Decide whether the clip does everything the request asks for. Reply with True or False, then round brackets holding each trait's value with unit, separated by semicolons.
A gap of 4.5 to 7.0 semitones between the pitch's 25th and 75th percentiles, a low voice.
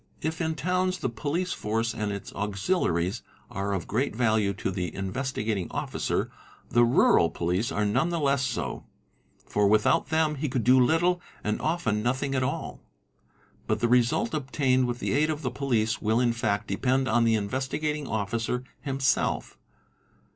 True (5.0 semitones; 120 Hz)